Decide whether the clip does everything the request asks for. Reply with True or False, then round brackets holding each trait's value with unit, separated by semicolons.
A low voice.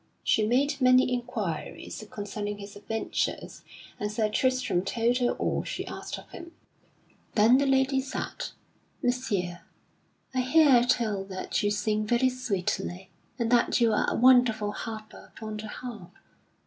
False (230 Hz)